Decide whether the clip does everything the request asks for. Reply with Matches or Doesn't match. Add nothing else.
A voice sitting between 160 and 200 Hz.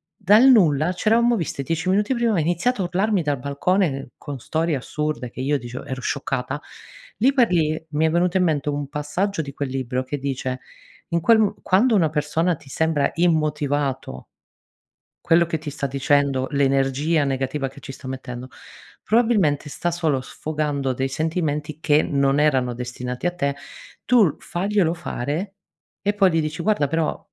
Doesn't match